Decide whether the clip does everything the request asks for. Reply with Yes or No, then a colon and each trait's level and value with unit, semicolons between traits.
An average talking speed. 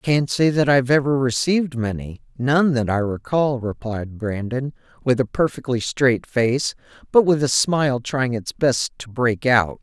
Yes: average, 175 wpm